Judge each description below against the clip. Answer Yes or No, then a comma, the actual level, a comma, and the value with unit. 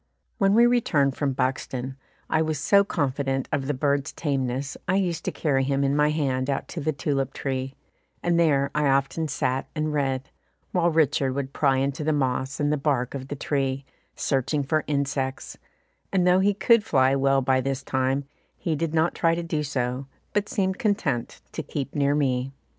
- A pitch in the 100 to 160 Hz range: Yes, medium, 140 Hz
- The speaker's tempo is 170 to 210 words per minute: Yes, average, 190 wpm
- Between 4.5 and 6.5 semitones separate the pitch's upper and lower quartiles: No, average, 2.9 semitones